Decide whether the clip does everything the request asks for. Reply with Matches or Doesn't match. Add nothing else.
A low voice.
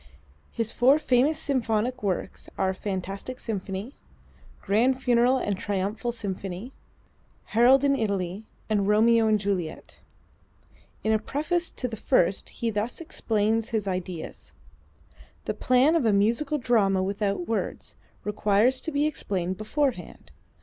Doesn't match